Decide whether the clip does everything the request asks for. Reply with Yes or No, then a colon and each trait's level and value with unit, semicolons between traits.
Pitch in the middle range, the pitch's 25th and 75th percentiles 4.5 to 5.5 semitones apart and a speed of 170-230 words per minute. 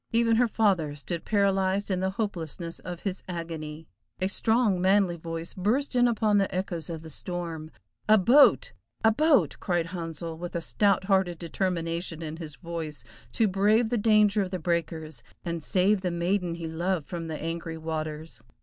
No: medium, 180 Hz; average, 3.5 semitones; average, 175 wpm